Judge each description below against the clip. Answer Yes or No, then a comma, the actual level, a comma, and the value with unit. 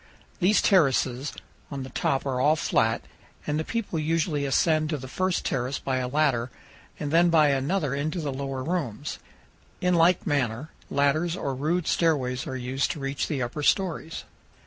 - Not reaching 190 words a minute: Yes, average, 170 wpm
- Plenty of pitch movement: No, average, 3.7 semitones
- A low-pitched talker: No, medium, 145 Hz